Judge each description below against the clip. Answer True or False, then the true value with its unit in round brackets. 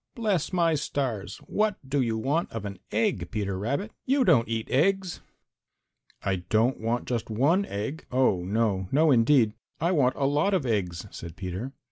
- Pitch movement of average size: False (7.1 semitones)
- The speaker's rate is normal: True (170 wpm)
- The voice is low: True (125 Hz)